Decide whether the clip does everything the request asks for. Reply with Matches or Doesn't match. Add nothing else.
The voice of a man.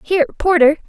Doesn't match